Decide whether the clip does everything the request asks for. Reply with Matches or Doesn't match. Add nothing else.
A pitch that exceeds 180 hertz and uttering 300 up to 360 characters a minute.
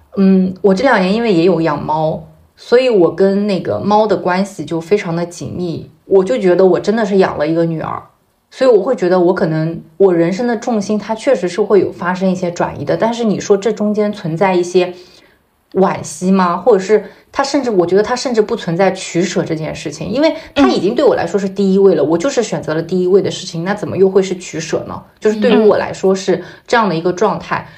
Matches